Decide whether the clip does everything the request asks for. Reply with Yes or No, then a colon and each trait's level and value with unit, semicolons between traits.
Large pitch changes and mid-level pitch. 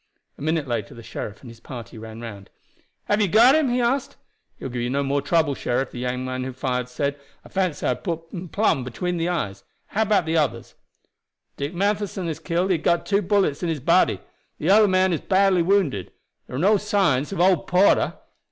Yes: wide, 7.2 semitones; medium, 165 Hz